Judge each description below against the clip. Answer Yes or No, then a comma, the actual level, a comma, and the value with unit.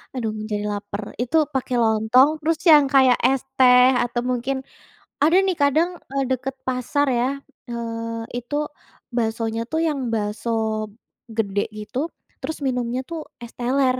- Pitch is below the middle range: No, very high, 250 Hz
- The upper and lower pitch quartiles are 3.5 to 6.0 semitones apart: No, average, 3.1 semitones